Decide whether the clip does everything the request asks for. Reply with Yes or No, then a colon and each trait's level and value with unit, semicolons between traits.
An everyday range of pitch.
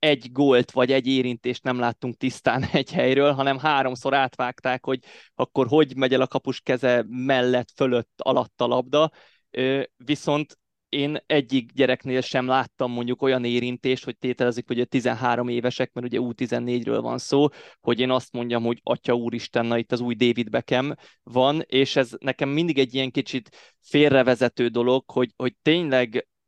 No: narrow, 1.7 semitones